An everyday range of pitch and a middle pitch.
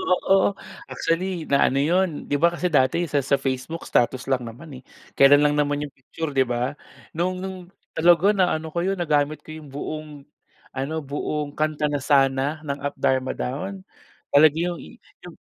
Yes: average, 3.6 semitones; medium, 150 Hz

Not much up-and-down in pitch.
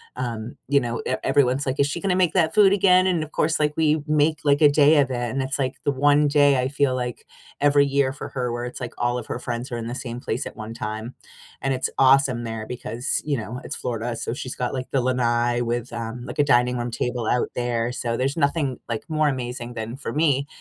No: average, 3.0 semitones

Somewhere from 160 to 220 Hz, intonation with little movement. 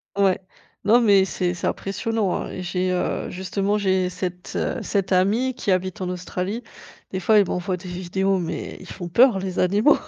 Yes: high, 190 Hz; narrow, 1.9 semitones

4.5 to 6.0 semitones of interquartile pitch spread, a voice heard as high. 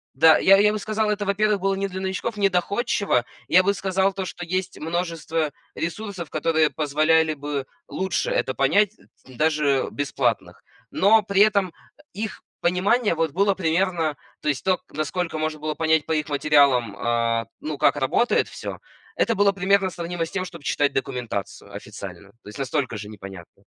No: average, 5.2 semitones; medium, 165 Hz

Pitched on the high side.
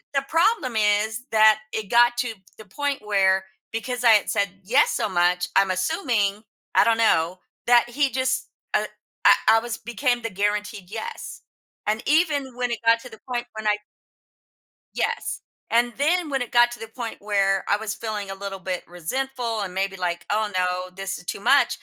Yes: high, 220 Hz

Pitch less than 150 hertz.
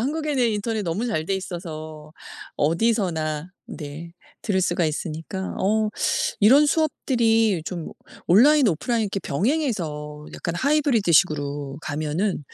No: high, 190 Hz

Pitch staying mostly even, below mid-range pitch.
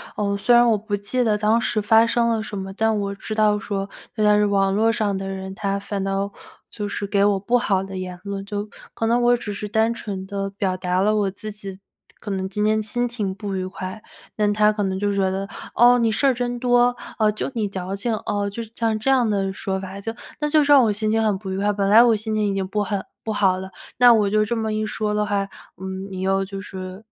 No: narrow, 2.2 semitones; high, 205 Hz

